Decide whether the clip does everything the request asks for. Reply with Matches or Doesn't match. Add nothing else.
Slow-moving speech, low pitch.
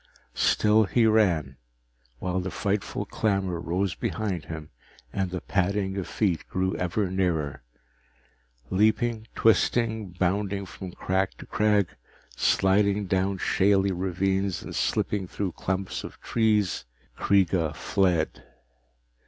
Matches